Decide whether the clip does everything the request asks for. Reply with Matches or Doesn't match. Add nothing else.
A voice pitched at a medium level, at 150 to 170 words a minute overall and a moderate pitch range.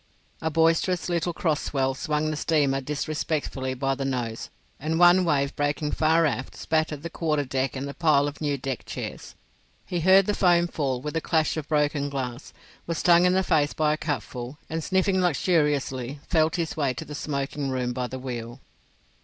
Doesn't match